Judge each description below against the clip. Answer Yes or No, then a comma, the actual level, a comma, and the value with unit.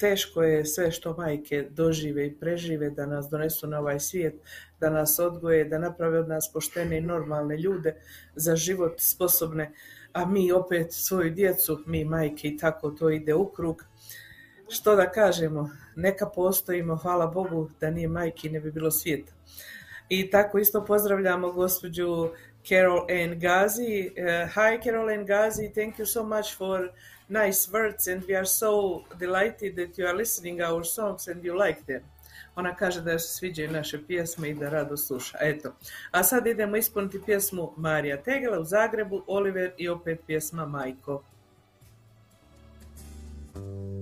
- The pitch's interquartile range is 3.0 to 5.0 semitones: Yes, average, 3.7 semitones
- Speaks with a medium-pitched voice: Yes, medium, 170 Hz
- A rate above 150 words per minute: Yes, fast, 160 wpm